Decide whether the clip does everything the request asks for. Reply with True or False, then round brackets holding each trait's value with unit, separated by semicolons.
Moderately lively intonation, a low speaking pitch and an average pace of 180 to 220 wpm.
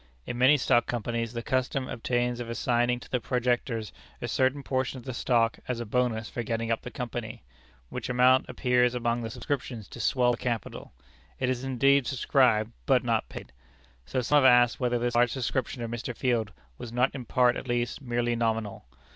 False (1.5 semitones; 120 Hz; 195 wpm)